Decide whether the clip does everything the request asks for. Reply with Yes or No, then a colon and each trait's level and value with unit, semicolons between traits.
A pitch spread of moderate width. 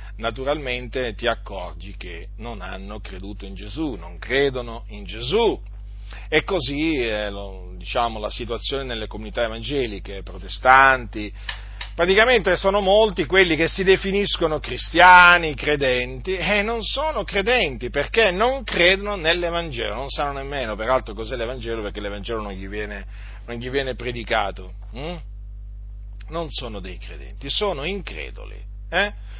No: wide, 8.3 semitones